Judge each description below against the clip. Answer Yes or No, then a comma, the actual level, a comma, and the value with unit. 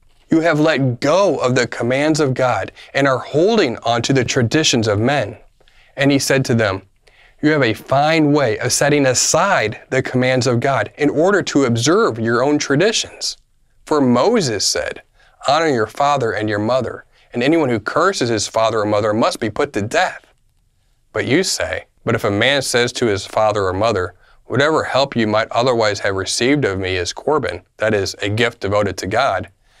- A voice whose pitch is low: Yes, low, 125 Hz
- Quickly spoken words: No, average, 190 wpm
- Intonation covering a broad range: No, average, 3.8 semitones